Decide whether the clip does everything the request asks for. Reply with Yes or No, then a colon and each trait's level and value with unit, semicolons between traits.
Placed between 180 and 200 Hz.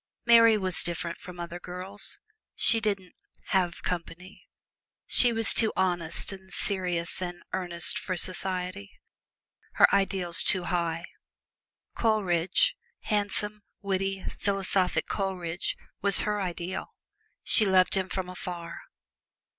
Yes: medium, 185 Hz